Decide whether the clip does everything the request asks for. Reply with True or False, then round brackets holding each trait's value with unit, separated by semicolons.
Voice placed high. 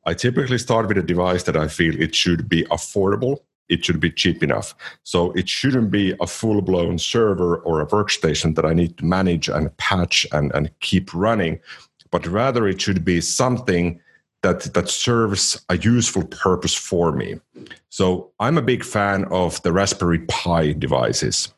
False (90 Hz)